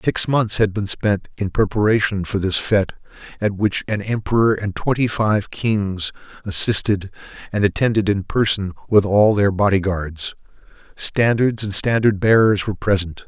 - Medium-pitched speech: No, low, 105 Hz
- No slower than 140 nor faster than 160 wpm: Yes, average, 155 wpm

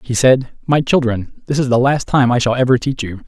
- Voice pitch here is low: Yes, low, 125 Hz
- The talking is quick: Yes, fast, 255 wpm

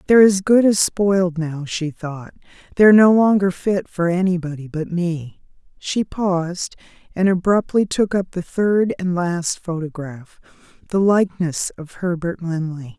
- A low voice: No, medium, 180 Hz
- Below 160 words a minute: Yes, average, 145 wpm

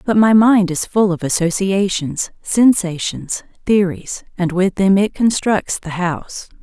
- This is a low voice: No, high, 190 Hz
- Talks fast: No, average, 145 wpm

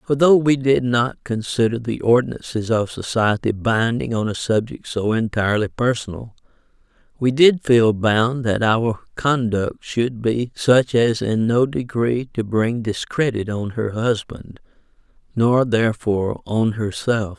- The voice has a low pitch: Yes, low, 115 Hz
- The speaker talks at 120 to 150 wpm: Yes, average, 140 wpm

